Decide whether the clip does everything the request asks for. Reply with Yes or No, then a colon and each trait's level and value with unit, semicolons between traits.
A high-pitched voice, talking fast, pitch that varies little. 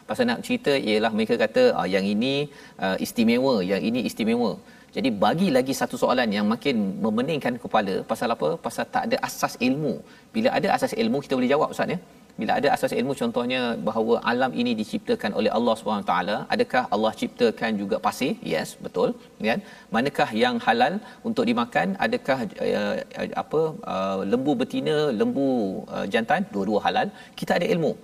Yes: high, 245 Hz; fast, 170 wpm; narrow, 2.1 semitones